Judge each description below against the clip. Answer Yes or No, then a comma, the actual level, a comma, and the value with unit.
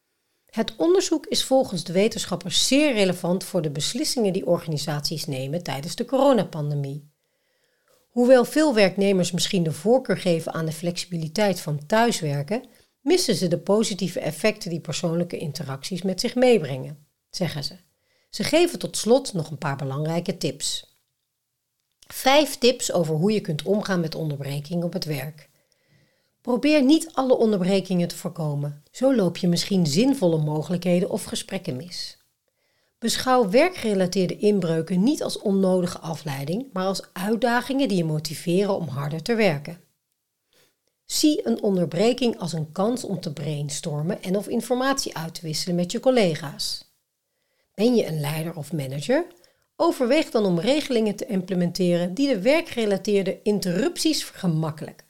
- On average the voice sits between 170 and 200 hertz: Yes, medium, 185 Hz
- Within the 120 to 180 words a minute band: Yes, average, 140 wpm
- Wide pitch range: Yes, wide, 6.5 semitones